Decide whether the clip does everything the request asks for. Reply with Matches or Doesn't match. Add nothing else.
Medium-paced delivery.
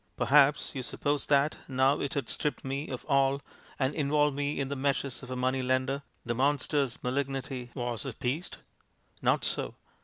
Matches